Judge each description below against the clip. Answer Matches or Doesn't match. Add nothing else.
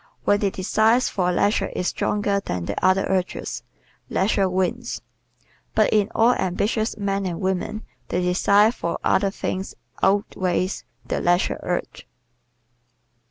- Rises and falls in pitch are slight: Matches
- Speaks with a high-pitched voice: Matches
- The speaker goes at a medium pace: Doesn't match